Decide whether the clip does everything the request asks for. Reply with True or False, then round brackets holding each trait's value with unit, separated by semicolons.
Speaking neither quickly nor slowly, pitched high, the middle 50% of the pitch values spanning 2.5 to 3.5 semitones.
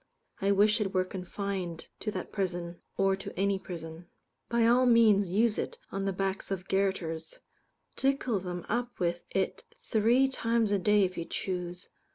True (170 wpm; 195 Hz; 3.1 semitones)